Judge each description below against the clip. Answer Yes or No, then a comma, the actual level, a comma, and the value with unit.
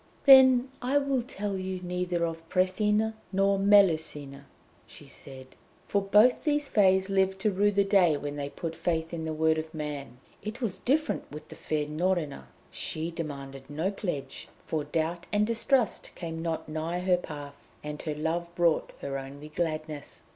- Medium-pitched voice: Yes, medium, 170 Hz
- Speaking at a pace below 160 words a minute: No, average, 170 wpm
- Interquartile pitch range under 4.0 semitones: No, average, 4.6 semitones